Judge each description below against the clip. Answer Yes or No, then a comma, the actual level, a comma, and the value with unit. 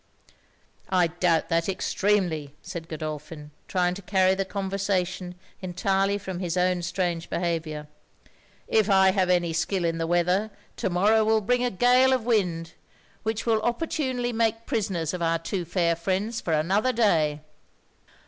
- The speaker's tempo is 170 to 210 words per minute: No, average, 150 wpm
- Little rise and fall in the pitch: No, average, 3.7 semitones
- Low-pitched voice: No, medium, 185 Hz